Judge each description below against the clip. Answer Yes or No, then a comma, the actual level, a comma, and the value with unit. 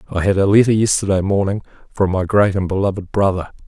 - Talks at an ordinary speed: Yes, average, 195 wpm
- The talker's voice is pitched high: No, low, 100 Hz